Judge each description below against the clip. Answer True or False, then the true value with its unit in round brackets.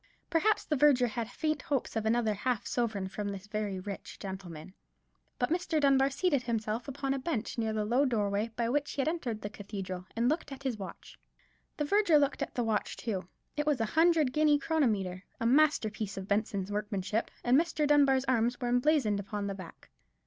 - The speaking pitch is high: True (240 Hz)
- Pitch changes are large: True (5.7 semitones)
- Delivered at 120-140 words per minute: False (195 wpm)